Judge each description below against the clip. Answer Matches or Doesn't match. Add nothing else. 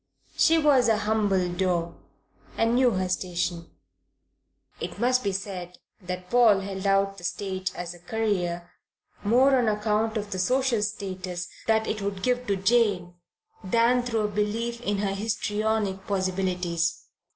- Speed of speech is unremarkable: Matches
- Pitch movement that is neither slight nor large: Matches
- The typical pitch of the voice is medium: Doesn't match